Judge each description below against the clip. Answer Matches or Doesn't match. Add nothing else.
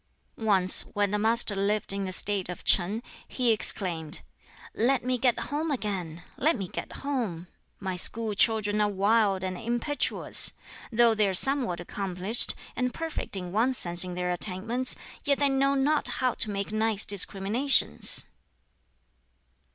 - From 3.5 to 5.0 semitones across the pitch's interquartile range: Matches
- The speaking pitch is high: Matches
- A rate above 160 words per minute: Doesn't match